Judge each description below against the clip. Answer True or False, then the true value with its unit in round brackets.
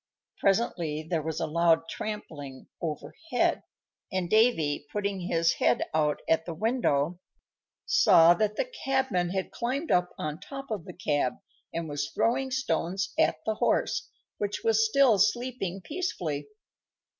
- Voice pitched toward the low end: False (185 Hz)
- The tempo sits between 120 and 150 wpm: True (140 wpm)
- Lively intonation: True (6.1 semitones)